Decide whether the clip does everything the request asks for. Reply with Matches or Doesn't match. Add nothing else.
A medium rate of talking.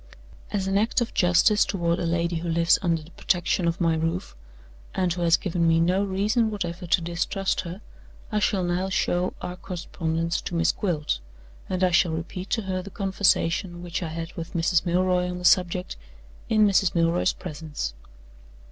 Matches